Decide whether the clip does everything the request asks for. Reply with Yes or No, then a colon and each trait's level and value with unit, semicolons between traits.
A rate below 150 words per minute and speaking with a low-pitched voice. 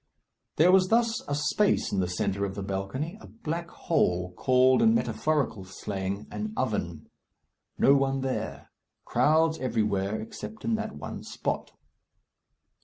Yes: average, 140 wpm; low, 130 Hz